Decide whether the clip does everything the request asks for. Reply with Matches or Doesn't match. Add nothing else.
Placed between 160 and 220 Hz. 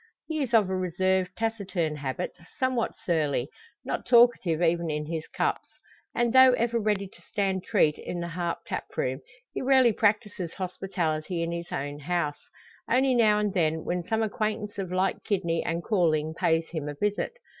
Matches